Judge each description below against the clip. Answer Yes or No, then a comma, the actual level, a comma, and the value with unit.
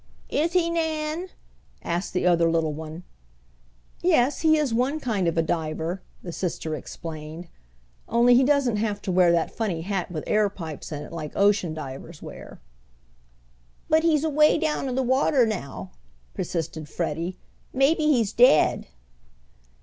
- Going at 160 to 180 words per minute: No, average, 150 wpm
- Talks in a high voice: Yes, high, 200 Hz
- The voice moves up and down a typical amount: No, wide, 9.0 semitones